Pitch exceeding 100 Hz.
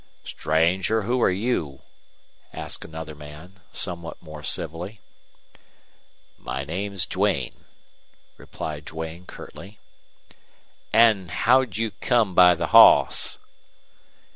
No: very low, 90 Hz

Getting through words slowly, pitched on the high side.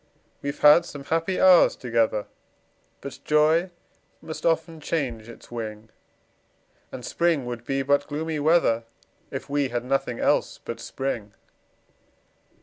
No: slow, 130 wpm; medium, 140 Hz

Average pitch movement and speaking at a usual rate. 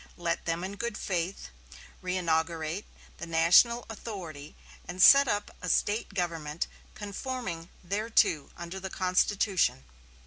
No: average, 3.7 semitones; slow, 115 wpm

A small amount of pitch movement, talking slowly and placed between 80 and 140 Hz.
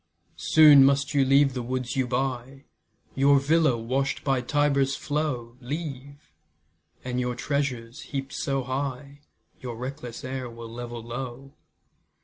Yes: narrow, 2.2 semitones; slow, 130 wpm; low, 135 Hz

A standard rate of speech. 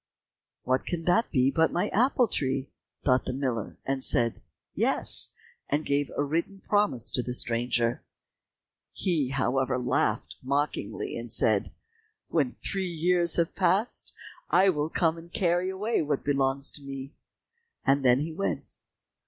Yes: average, 145 wpm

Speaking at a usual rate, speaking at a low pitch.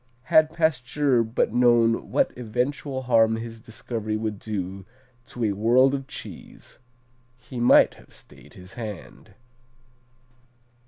No: slow, 120 wpm; low, 115 Hz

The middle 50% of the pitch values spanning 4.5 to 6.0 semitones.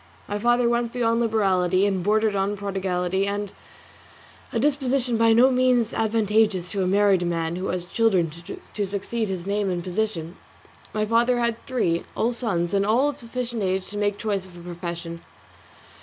No: average, 3.8 semitones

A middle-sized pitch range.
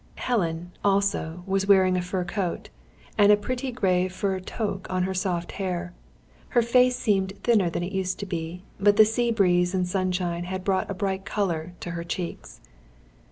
No: narrow, 2.2 semitones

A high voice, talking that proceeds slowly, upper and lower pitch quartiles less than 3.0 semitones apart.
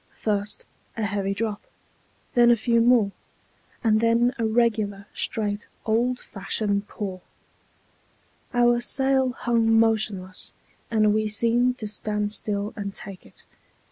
Yes: high, 220 Hz; slow, 125 wpm; narrow, 2.5 semitones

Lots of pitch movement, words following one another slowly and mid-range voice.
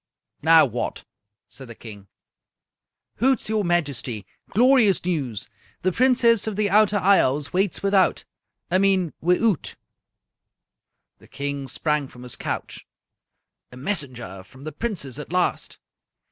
Yes: wide, 7.1 semitones; slow, 125 wpm; medium, 170 Hz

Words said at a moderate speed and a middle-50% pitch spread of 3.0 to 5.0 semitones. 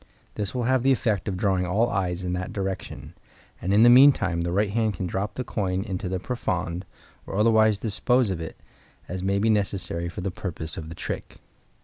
No: fast, 210 wpm; average, 3.3 semitones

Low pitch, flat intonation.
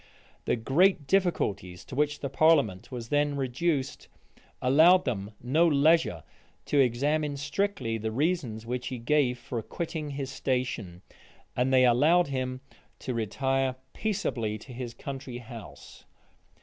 No: low, 130 Hz; average, 4.0 semitones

